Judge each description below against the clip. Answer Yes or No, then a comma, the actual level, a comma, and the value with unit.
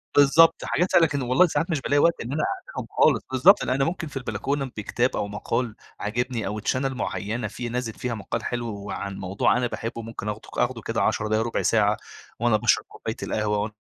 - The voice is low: Yes, low, 120 Hz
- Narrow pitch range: No, average, 4.1 semitones